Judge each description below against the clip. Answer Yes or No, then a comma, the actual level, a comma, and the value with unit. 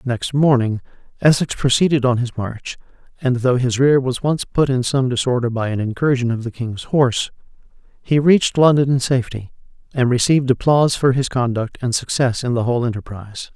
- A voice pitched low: Yes, low, 125 Hz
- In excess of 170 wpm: Yes, average, 180 wpm